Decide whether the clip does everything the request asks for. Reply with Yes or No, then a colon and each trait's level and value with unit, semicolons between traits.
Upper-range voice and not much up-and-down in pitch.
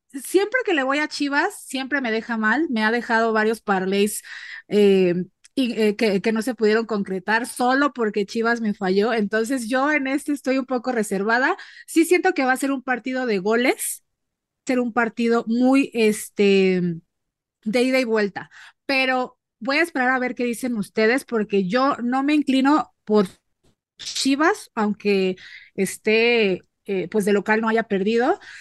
No: high, 235 Hz; average, 4.0 semitones